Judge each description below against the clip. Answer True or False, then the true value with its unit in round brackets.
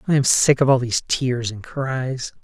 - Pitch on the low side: True (130 Hz)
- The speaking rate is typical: False (220 wpm)